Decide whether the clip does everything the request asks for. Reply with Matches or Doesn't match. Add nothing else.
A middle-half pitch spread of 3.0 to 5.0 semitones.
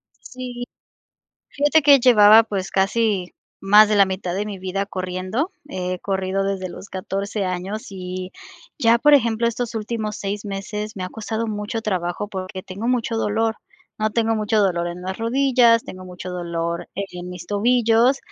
Matches